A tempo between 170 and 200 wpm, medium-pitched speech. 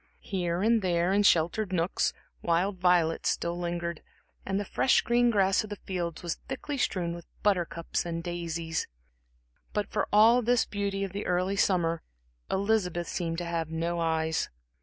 No: average, 160 wpm; medium, 180 Hz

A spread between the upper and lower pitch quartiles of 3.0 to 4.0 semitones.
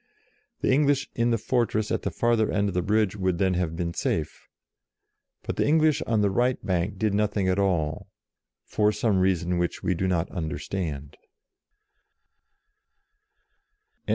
Yes: average, 3.7 semitones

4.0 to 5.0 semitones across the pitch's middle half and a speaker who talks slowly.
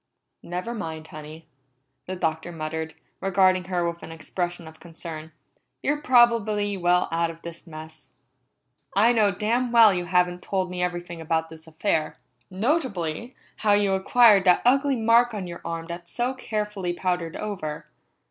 No: average, 4.3 semitones; average, 155 wpm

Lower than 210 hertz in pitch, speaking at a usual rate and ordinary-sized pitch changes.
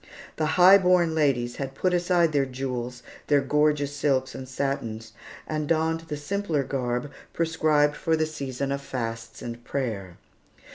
Yes: medium, 140 Hz; average, 150 wpm; average, 3.7 semitones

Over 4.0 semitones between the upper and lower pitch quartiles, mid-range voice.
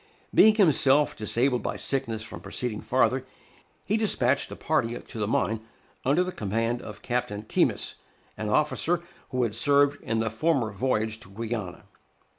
No: average, 4.5 semitones; low, 120 Hz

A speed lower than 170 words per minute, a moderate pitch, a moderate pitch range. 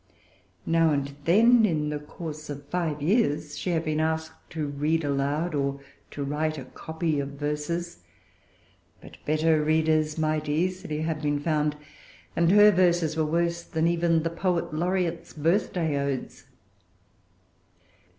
No: average, 140 wpm; medium, 155 Hz; narrow, 2.3 semitones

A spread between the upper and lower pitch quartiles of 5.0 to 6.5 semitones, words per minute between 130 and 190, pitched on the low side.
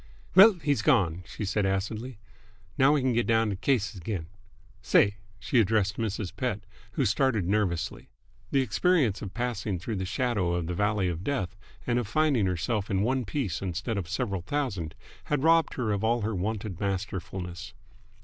No: average, 4.6 semitones; average, 175 wpm; low, 105 Hz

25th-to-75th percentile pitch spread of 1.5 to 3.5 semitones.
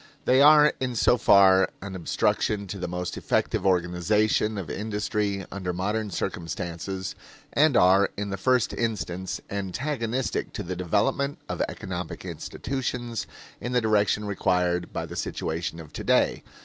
No: average, 4.1 semitones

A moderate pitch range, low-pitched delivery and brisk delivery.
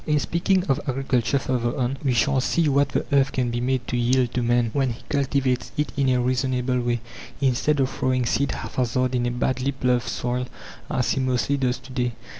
No: narrow, 1.8 semitones; low, 130 Hz; fast, 210 wpm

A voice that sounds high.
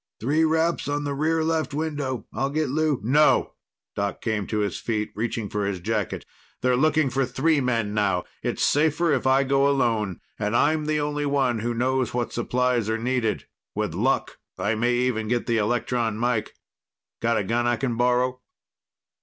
No: low, 125 Hz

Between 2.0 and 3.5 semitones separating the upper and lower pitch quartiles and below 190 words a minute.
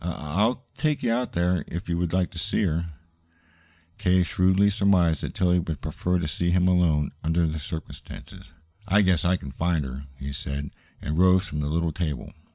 No: average, 2.9 semitones; average, 195 wpm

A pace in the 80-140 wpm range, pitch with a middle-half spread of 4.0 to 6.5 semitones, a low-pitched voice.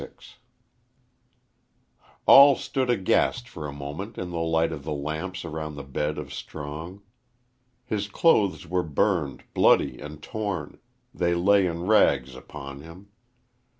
Yes: slow, 135 wpm; average, 4.9 semitones; very low, 85 Hz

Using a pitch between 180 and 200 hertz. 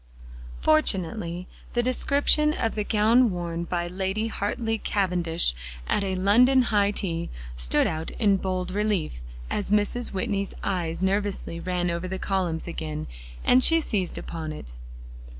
Yes: high, 190 Hz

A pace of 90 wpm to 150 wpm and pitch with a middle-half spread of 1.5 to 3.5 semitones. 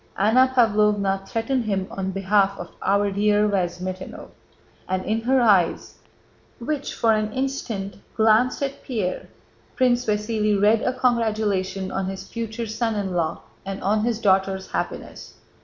Yes: average, 140 wpm; average, 3.0 semitones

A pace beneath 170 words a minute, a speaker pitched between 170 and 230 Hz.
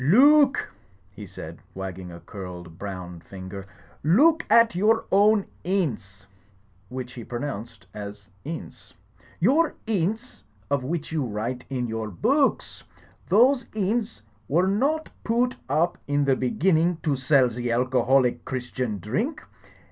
No: average, 140 wpm; low, 135 Hz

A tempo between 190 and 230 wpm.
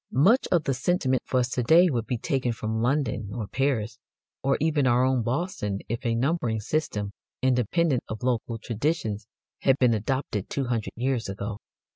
No: average, 175 wpm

